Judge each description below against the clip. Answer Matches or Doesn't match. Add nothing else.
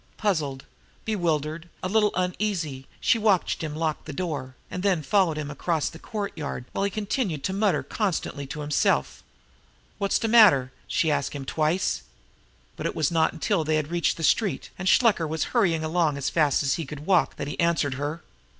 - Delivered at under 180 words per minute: Doesn't match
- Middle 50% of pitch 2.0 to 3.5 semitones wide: Doesn't match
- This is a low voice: Doesn't match